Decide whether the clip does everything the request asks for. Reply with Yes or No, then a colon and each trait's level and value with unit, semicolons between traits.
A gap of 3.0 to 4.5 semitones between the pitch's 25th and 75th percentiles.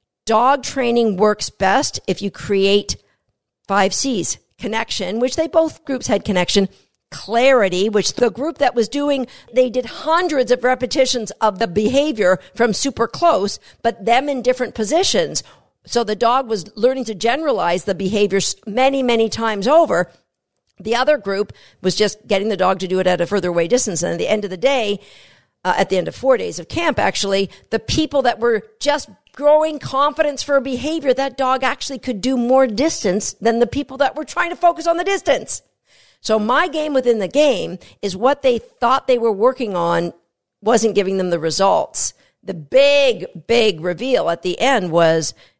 No: average, 5.3 semitones